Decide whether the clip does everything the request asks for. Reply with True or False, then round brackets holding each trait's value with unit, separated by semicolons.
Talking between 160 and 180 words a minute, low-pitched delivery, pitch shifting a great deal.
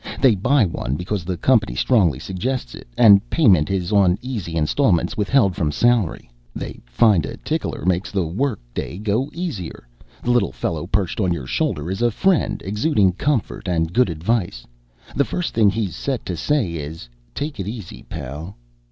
True (175 wpm; 100 Hz; 6.1 semitones)